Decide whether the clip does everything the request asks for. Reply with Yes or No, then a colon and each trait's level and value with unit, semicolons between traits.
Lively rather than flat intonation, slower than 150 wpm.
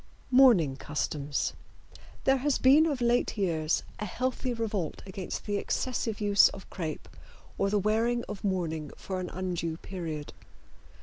Yes: wide, 6.0 semitones; average, 140 wpm